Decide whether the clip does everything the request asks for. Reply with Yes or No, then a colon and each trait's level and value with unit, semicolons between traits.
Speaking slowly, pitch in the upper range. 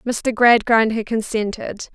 Yes: slow, 125 wpm; high, 225 Hz